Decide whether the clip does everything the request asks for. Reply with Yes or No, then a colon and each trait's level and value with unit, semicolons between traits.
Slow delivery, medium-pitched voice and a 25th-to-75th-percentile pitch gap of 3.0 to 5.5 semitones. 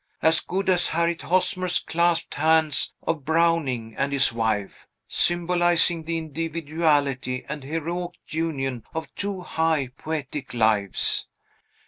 Yes: slow, 115 wpm; medium, 160 Hz; average, 3.6 semitones